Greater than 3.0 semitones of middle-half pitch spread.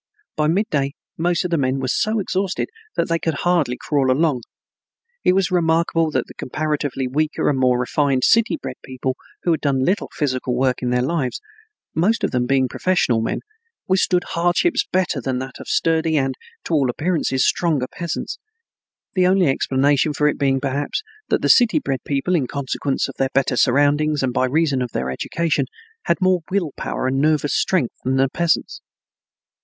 Yes: average, 4.4 semitones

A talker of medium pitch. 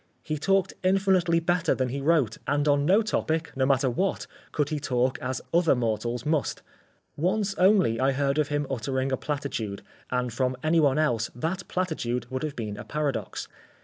Yes: medium, 145 Hz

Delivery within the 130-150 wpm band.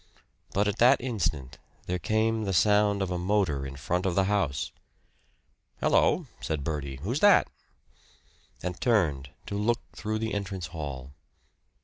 Yes: average, 145 wpm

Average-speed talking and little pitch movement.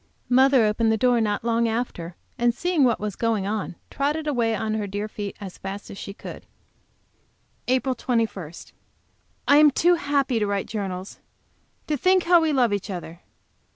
No: average, 175 wpm; average, 4.9 semitones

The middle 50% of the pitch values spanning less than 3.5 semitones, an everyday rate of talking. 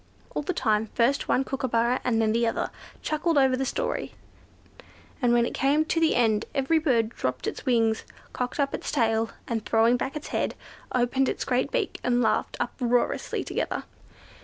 Yes: average, 3.1 semitones; average, 175 wpm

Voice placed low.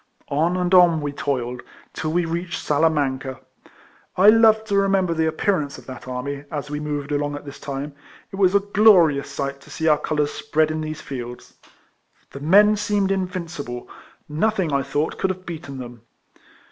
No: medium, 155 Hz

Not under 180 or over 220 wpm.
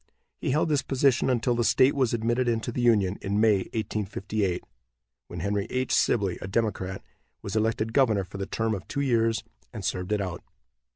Yes: average, 185 wpm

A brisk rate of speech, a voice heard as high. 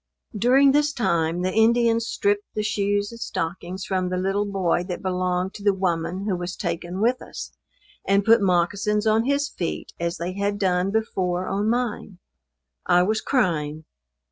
No: average, 170 wpm; high, 195 Hz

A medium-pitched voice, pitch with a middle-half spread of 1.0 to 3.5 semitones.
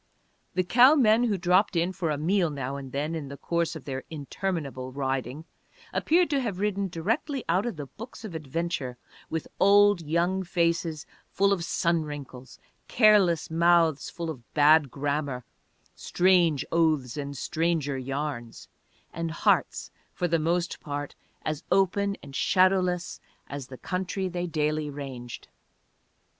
No: medium, 165 Hz; average, 4.5 semitones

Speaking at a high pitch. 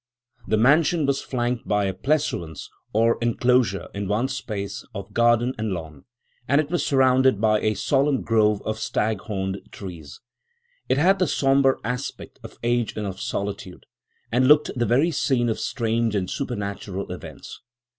No: low, 115 Hz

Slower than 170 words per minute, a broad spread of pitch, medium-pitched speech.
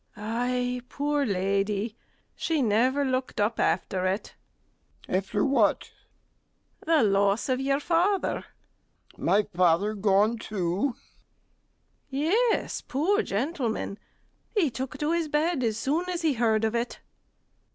No: average, 140 wpm; wide, 6.0 semitones; high, 245 Hz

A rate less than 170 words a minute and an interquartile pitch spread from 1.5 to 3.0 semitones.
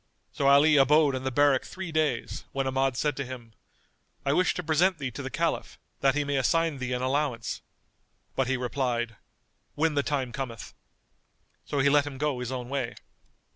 No: average, 190 wpm; narrow, 2.5 semitones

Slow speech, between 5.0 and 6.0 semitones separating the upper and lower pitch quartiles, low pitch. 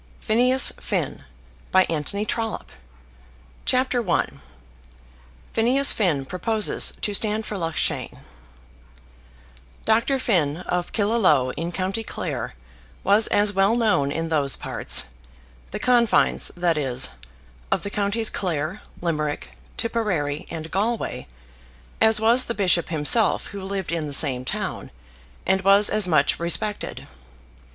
No: slow, 120 wpm; wide, 5.4 semitones; high, 195 Hz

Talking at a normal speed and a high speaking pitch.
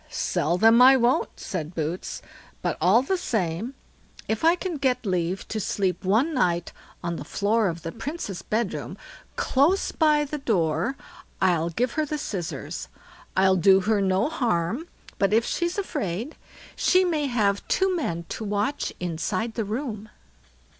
Yes: average, 155 wpm; high, 220 Hz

